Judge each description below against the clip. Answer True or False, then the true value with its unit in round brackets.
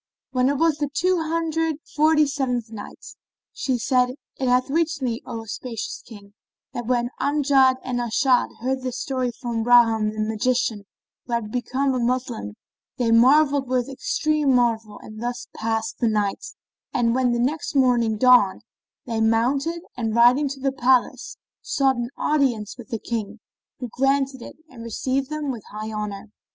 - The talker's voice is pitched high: True (250 Hz)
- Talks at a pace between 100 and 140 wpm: False (165 wpm)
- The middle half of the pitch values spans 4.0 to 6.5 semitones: False (3.1 semitones)